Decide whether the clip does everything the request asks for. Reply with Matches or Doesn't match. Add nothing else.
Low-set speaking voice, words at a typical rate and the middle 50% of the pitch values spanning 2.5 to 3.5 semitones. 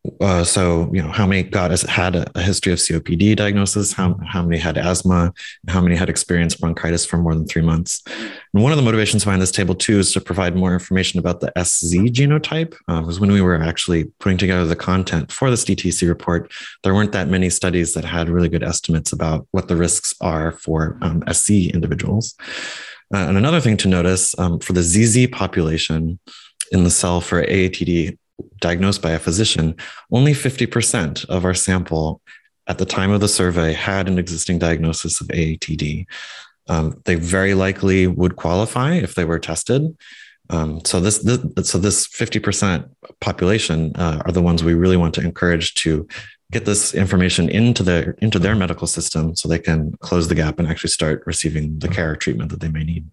Matches